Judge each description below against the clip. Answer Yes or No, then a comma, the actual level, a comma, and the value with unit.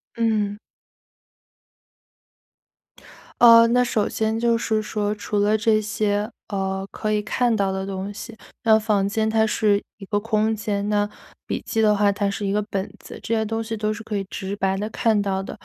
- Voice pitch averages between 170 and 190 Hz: No, high, 210 Hz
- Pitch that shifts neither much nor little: No, narrow, 1.6 semitones